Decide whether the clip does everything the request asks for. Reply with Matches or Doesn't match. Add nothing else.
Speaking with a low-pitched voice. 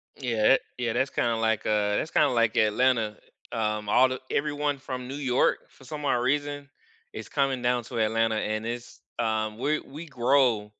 Matches